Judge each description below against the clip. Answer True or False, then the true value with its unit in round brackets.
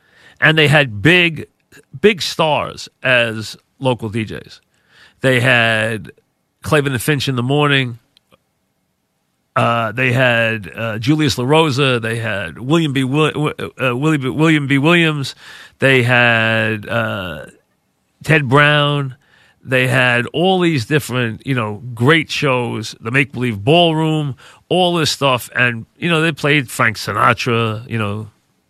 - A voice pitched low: True (130 Hz)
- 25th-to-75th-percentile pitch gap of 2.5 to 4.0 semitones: False (4.7 semitones)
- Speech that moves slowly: True (130 wpm)